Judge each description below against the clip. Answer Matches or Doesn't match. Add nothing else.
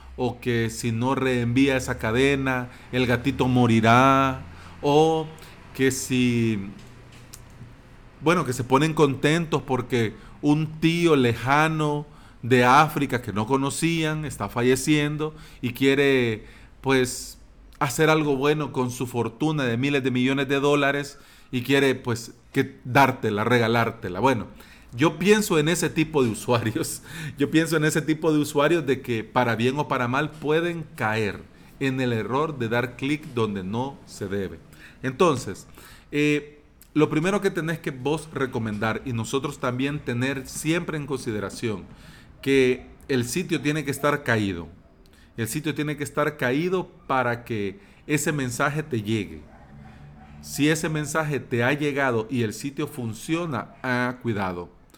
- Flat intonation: Doesn't match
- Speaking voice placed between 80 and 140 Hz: Matches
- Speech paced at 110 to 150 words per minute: Matches